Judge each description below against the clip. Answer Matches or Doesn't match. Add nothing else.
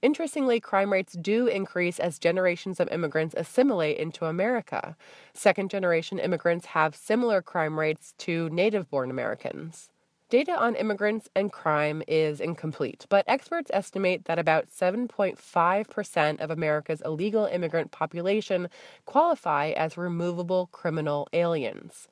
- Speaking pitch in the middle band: Matches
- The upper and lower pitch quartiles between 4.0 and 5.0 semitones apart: Matches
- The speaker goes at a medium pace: Doesn't match